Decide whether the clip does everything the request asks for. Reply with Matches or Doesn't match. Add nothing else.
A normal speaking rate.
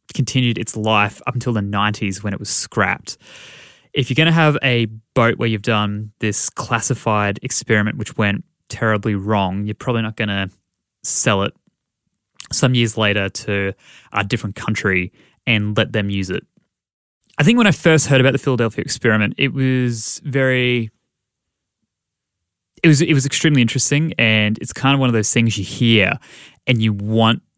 Matches